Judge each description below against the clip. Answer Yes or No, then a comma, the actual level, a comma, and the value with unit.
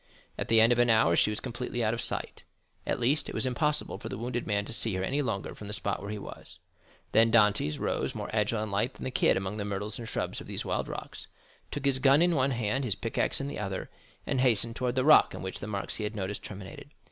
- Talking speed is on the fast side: Yes, fast, 265 wpm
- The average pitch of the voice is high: No, low, 115 Hz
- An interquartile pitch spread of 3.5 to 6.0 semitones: Yes, average, 3.8 semitones